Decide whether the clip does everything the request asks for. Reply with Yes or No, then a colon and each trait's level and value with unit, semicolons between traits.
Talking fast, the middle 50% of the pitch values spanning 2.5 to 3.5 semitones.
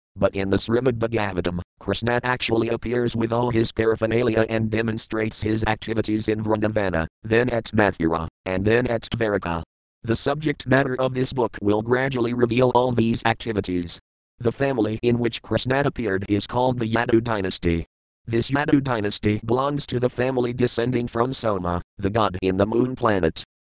No: average, 165 wpm; average, 2.9 semitones